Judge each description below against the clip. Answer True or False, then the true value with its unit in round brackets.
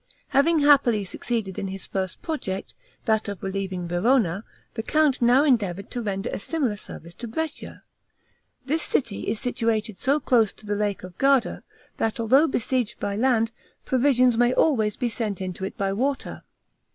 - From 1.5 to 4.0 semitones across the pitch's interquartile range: False (4.8 semitones)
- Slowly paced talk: False (165 wpm)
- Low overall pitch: False (225 Hz)